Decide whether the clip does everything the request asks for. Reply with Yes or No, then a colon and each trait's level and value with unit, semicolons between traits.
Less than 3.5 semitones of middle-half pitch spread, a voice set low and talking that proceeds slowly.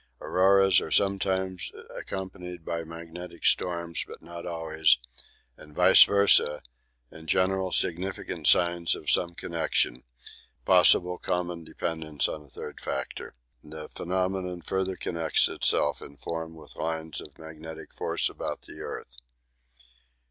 Yes: narrow, 2.5 semitones; very low, 85 Hz; slow, 125 wpm